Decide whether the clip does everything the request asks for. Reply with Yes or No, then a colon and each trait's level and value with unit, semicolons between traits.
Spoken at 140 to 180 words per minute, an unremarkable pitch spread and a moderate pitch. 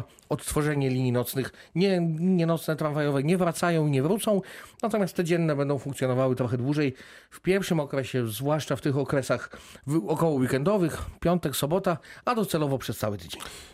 Yes: average, 155 wpm; average, 4.8 semitones; medium, 150 Hz